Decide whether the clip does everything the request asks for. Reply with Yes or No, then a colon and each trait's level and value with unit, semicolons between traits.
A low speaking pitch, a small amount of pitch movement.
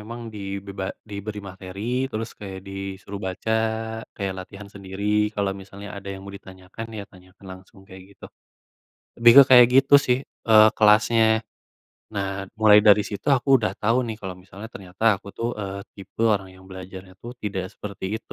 Yes: low, 100 Hz; narrow, 2.1 semitones